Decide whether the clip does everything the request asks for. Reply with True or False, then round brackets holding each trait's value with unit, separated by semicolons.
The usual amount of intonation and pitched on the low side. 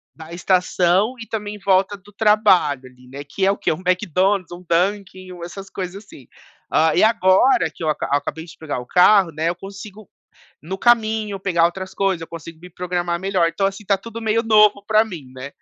False (3.4 semitones; 185 Hz)